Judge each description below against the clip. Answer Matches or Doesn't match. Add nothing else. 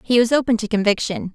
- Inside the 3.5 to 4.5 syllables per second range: Doesn't match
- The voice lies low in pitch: Doesn't match